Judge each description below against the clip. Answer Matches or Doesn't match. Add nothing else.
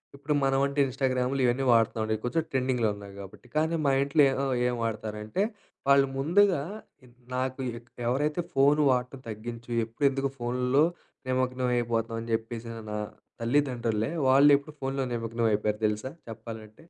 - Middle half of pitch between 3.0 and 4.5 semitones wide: Matches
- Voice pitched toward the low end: Matches